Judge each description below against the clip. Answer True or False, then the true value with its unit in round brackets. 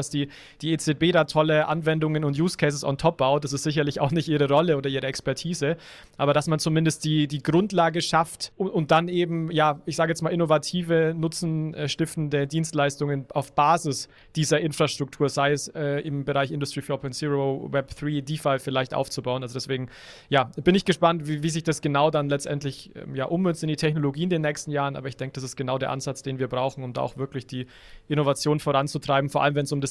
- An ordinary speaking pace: False (210 wpm)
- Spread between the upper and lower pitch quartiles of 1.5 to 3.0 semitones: True (2.4 semitones)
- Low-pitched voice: False (150 Hz)